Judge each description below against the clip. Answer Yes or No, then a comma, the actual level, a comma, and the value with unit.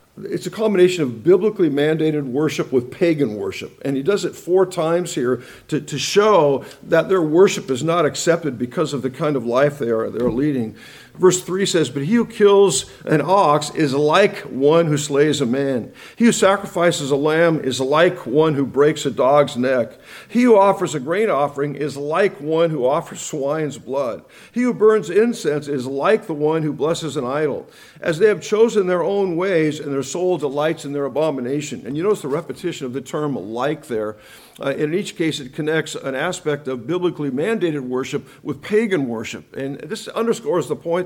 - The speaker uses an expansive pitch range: No, average, 4.5 semitones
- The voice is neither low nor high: Yes, medium, 155 Hz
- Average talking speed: Yes, average, 195 wpm